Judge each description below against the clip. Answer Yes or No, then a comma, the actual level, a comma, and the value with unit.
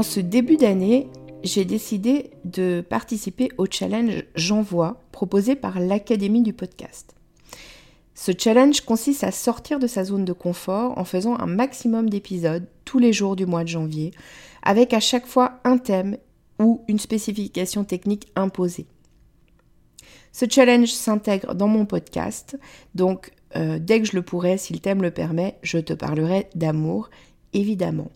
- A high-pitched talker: Yes, high, 205 Hz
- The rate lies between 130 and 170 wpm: Yes, average, 155 wpm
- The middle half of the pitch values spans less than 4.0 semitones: No, average, 4.3 semitones